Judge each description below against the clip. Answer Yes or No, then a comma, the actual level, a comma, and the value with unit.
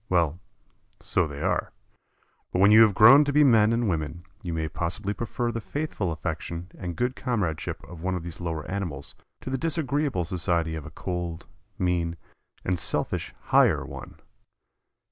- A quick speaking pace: No, average, 165 wpm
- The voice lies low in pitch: Yes, very low, 90 Hz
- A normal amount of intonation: No, wide, 5.7 semitones